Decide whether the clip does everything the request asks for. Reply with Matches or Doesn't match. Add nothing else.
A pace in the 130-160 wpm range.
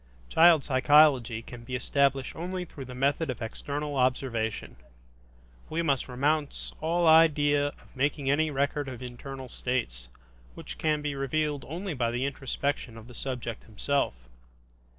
Matches